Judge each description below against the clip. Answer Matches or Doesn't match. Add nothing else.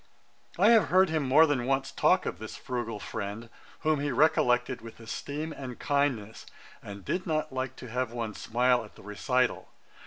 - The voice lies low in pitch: Matches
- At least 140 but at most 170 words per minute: Doesn't match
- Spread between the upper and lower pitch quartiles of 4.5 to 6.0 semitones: Doesn't match